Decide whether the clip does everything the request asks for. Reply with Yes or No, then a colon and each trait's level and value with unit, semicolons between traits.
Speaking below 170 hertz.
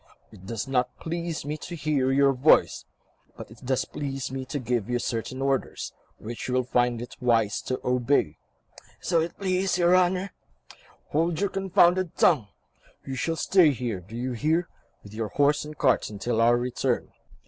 Yes: low, 135 Hz